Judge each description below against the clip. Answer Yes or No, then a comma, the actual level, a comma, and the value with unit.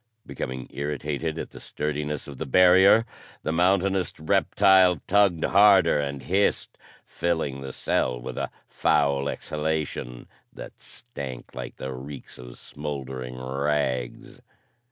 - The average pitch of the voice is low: Yes, very low, 75 Hz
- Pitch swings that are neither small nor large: Yes, average, 5.0 semitones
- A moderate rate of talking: No, slow, 120 wpm